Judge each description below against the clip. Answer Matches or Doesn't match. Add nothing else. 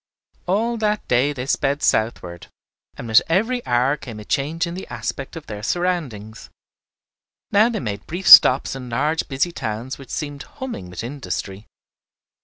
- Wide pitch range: Matches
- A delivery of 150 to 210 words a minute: Matches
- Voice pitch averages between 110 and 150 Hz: Matches